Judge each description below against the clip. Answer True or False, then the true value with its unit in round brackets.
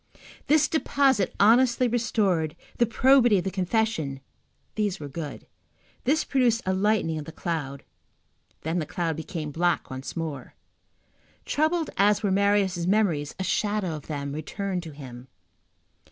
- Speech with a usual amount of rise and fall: False (5.9 semitones)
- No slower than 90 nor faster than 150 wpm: True (140 wpm)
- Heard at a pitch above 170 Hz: True (190 Hz)